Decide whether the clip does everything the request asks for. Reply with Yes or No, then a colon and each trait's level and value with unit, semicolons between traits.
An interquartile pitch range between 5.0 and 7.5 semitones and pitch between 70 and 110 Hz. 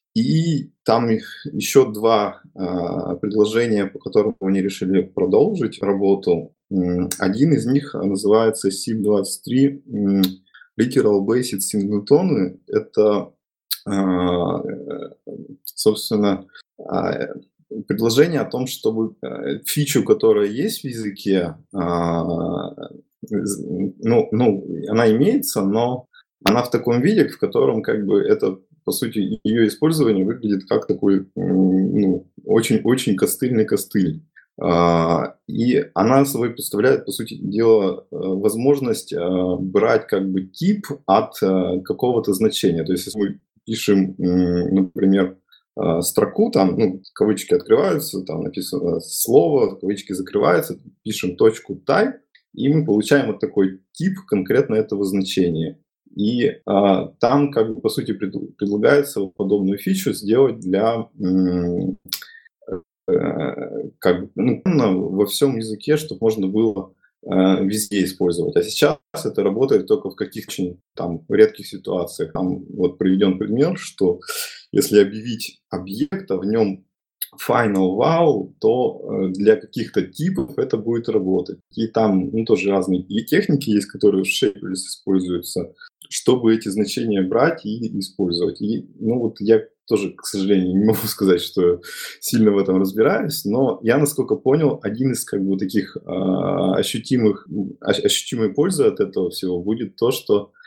Yes: wide, 5.4 semitones; low, 105 Hz